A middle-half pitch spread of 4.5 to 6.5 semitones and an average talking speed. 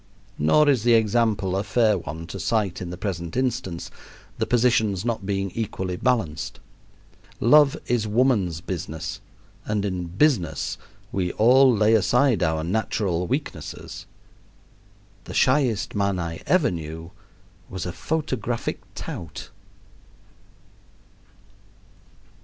No: average, 5.3 semitones; slow, 115 wpm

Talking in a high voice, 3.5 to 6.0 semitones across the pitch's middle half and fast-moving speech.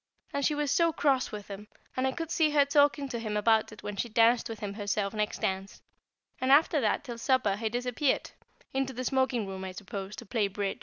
Yes: high, 235 Hz; average, 4.6 semitones; fast, 225 wpm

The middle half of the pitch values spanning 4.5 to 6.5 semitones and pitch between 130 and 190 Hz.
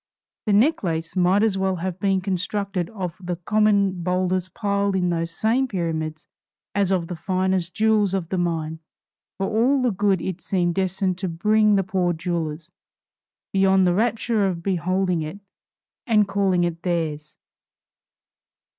No: average, 2.7 semitones; medium, 185 Hz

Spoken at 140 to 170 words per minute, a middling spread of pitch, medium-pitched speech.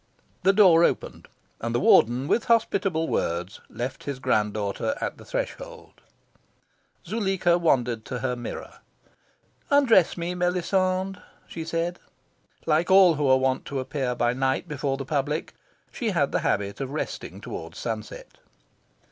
No: average, 145 wpm; wide, 6.4 semitones; medium, 155 Hz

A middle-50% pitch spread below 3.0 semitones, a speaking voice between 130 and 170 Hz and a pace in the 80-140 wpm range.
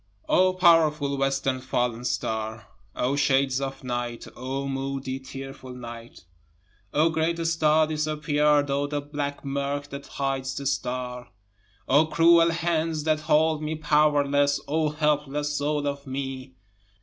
Yes: narrow, 2.4 semitones; medium, 140 Hz; slow, 135 wpm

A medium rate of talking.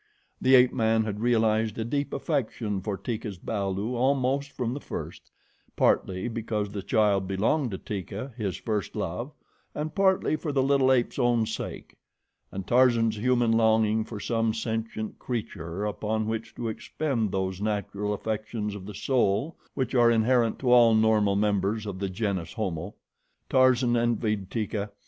Yes: average, 155 wpm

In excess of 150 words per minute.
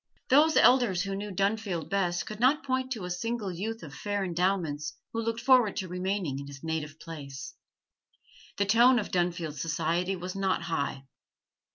Yes: average, 170 wpm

